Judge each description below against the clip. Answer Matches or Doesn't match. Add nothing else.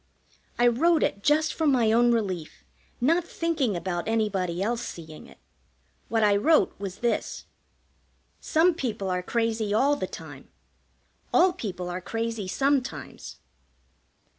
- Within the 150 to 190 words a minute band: Doesn't match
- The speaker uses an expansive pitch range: Matches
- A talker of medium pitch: Doesn't match